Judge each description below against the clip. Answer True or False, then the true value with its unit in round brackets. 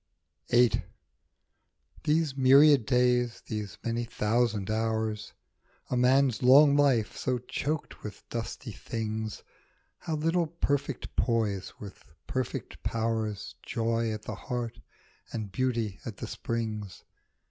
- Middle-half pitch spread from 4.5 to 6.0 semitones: False (3.0 semitones)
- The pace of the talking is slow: True (120 wpm)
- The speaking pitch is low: True (115 Hz)